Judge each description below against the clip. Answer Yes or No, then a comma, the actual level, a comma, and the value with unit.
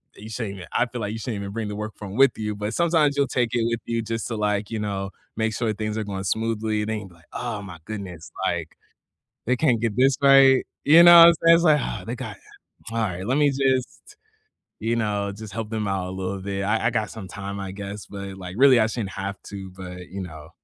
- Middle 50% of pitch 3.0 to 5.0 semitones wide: Yes, average, 3.3 semitones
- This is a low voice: Yes, low, 110 Hz